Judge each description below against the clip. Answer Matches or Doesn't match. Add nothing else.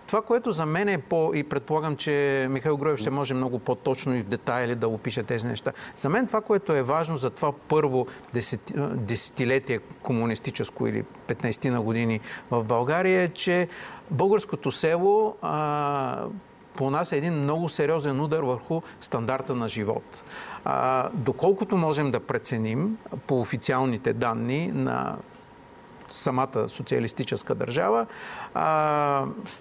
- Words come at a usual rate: Matches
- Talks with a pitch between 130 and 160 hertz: Matches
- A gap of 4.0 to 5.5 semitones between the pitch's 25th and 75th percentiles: Matches